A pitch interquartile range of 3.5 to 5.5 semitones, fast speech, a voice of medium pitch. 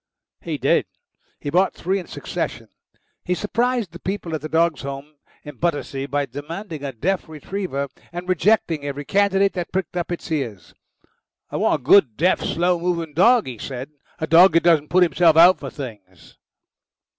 No: average, 4.3 semitones; average, 175 wpm; medium, 165 Hz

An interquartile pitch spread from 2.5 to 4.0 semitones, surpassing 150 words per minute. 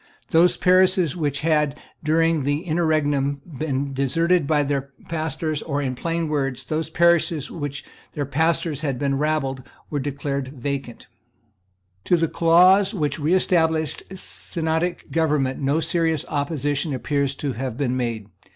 No: average, 3.0 semitones; average, 140 wpm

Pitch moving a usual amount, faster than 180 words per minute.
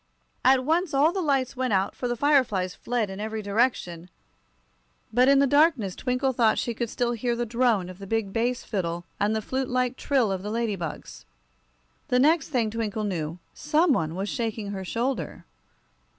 Yes: average, 4.5 semitones; average, 190 wpm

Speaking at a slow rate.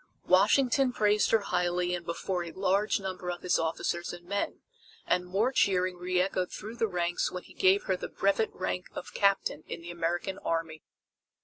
No: average, 180 wpm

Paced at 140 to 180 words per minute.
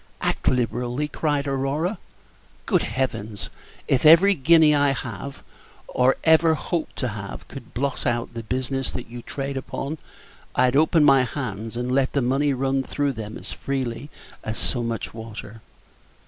Yes: average, 155 wpm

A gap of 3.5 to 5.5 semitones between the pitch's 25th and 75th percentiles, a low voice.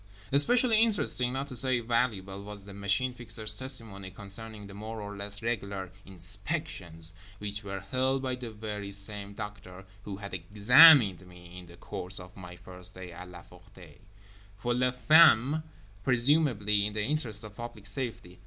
Yes: average, 4.4 semitones; low, 105 Hz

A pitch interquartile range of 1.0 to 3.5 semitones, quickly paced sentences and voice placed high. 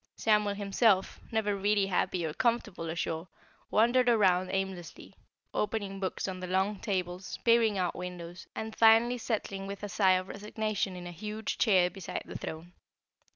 No: average, 2.9 semitones; average, 155 wpm; high, 195 Hz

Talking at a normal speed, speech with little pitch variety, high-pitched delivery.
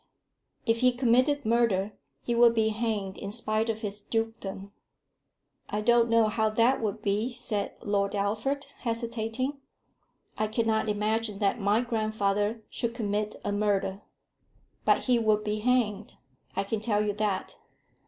Yes: average, 145 wpm; narrow, 2.1 semitones; high, 220 Hz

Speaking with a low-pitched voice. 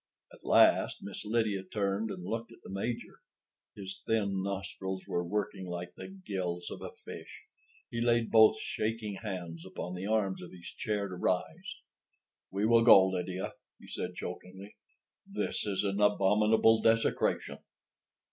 Yes: low, 100 Hz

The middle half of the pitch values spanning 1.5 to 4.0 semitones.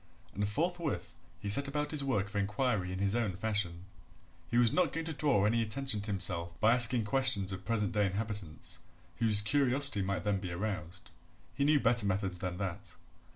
No: average, 4.7 semitones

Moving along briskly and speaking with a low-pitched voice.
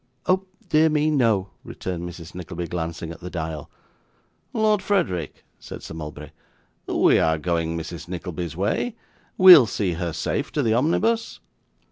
No: average, 145 wpm; very low, 90 Hz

